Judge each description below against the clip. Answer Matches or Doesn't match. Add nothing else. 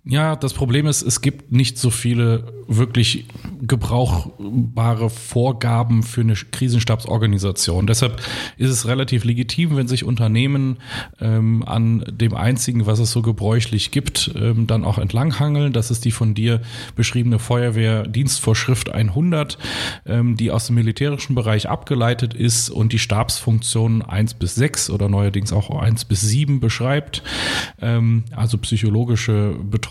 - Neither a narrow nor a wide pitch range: Doesn't match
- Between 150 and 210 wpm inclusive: Doesn't match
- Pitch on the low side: Matches